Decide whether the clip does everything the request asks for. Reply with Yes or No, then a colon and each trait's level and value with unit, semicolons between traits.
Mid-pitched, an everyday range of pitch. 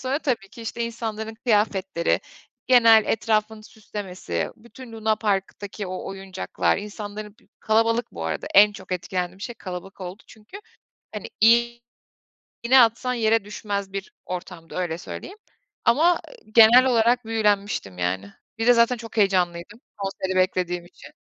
No: high, 210 Hz; average, 3.4 semitones